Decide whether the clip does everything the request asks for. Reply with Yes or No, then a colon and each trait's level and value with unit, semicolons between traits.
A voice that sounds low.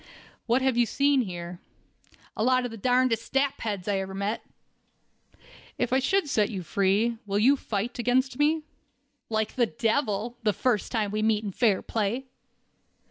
No: high, 230 Hz